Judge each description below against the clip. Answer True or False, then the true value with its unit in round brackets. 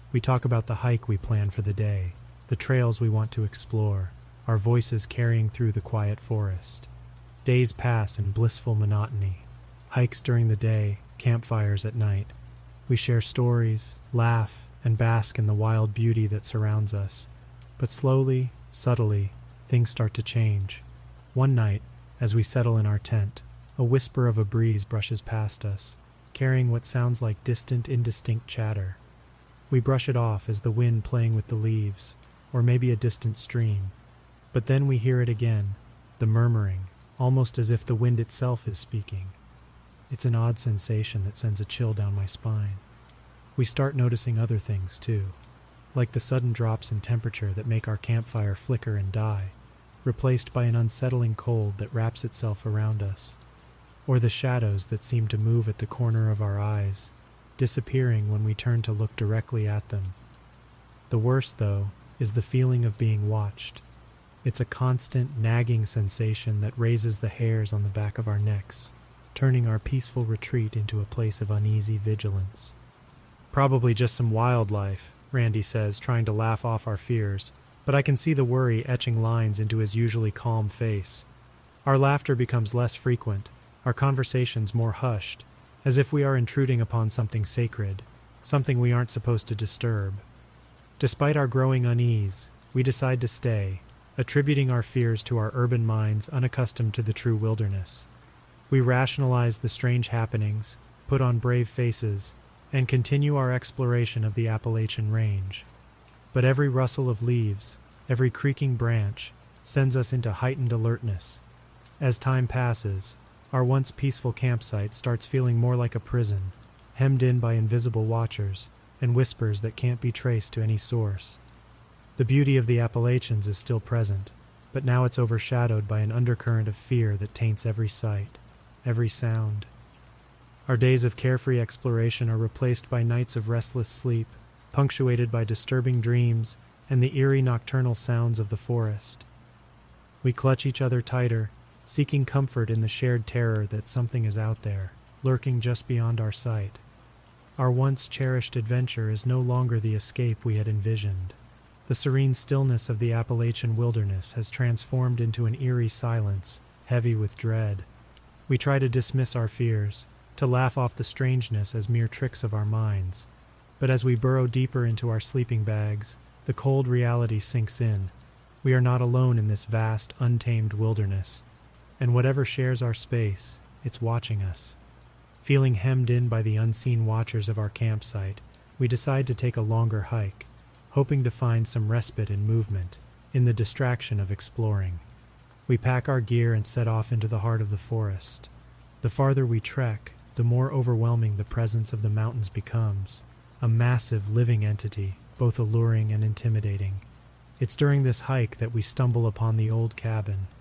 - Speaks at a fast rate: False (165 wpm)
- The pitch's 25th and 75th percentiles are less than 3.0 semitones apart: True (2.4 semitones)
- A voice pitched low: True (115 Hz)